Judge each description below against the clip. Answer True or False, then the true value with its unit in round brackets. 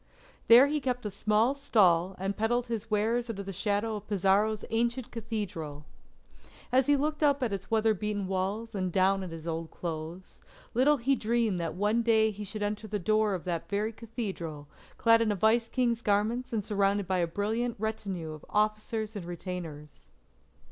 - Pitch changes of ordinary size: True (3.4 semitones)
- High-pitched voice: True (210 Hz)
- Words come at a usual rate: True (180 wpm)